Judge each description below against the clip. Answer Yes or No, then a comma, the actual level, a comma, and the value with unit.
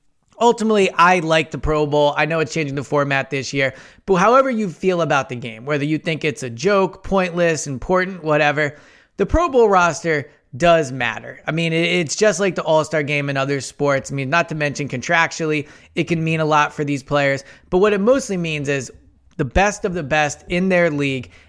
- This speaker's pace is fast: Yes, fast, 210 wpm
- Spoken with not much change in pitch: No, average, 3.8 semitones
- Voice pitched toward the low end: No, medium, 155 Hz